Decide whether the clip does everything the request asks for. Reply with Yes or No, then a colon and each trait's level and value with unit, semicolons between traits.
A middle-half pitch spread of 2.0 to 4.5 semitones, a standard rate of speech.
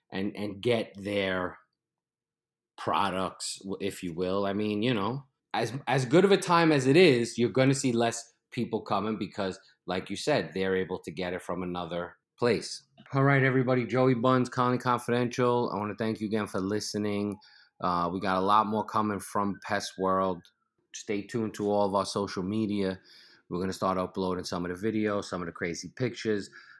Yes: average, 4.1 semitones; average, 190 wpm